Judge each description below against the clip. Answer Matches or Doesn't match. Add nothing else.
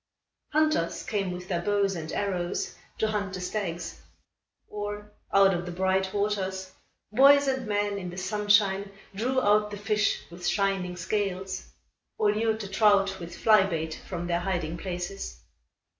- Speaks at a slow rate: Doesn't match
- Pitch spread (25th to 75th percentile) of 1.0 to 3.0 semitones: Matches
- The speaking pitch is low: Doesn't match